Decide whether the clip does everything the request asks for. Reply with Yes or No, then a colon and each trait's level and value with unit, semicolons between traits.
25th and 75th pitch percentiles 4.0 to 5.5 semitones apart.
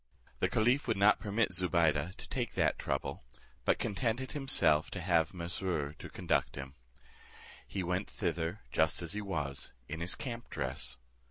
Yes: average, 4.8 semitones